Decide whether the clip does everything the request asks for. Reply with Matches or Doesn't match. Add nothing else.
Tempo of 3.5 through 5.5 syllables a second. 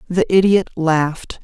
Matches